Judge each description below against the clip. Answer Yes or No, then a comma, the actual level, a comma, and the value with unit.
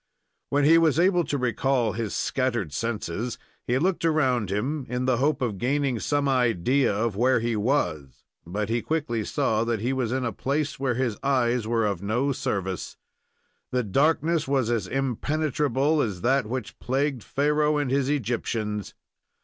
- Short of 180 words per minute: Yes, average, 165 wpm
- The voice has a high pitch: No, low, 125 Hz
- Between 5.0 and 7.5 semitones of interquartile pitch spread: No, average, 3.9 semitones